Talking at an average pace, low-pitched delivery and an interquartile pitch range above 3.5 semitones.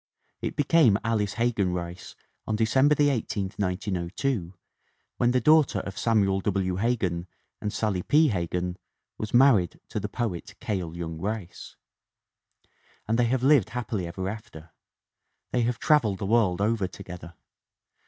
Yes: average, 145 wpm; low, 105 Hz; average, 4.7 semitones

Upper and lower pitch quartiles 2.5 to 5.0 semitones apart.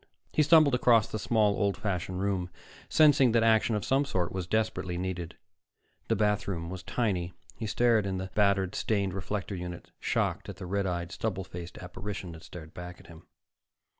Yes: average, 3.5 semitones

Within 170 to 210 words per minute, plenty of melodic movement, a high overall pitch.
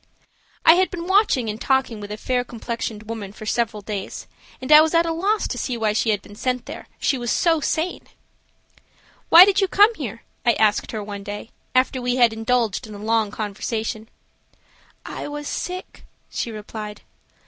Yes: average, 190 wpm; wide, 5.9 semitones; high, 235 Hz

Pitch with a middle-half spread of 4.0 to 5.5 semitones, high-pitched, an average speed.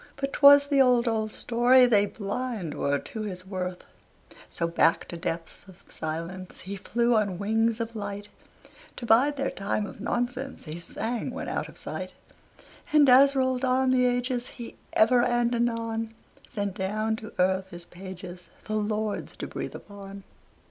Yes: average, 4.5 semitones; high, 220 Hz; average, 165 wpm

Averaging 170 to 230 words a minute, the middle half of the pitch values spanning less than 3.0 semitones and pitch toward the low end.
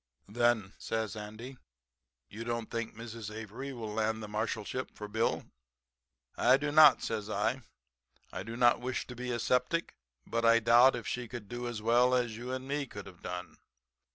Yes: average, 180 wpm; narrow, 2.4 semitones; low, 115 Hz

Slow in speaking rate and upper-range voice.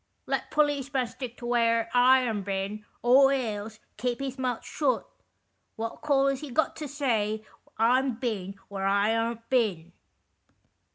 No: average, 150 wpm; high, 240 Hz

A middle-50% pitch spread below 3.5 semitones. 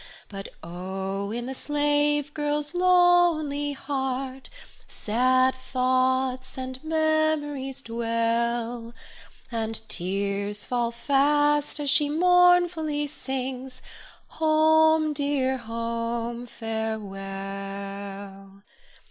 No: average, 4.5 semitones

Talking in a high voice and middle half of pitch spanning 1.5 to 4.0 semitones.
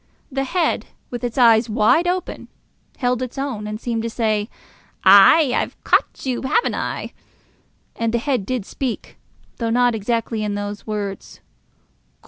Yes: high, 235 Hz; average, 3.2 semitones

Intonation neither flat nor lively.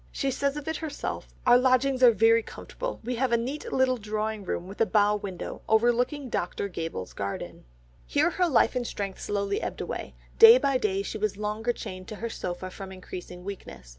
Yes: average, 4.5 semitones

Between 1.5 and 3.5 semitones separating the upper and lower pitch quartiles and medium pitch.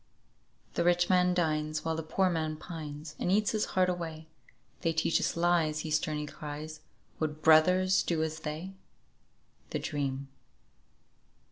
Yes: narrow, 2.4 semitones; medium, 160 Hz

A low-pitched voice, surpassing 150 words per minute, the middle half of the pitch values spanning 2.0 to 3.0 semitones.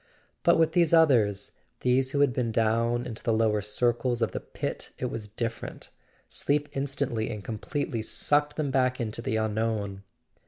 No: low, 120 Hz; average, 165 wpm; average, 3.7 semitones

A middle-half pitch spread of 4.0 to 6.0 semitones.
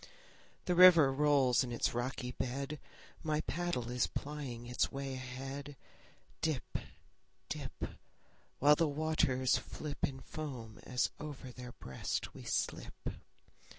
No: average, 3.1 semitones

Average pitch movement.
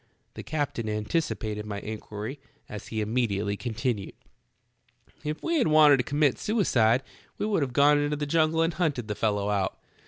No: wide, 6.2 semitones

